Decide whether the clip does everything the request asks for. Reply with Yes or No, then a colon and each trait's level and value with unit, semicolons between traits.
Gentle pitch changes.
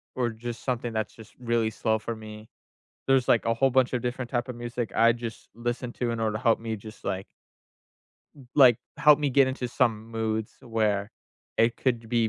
Yes: narrow, 1.9 semitones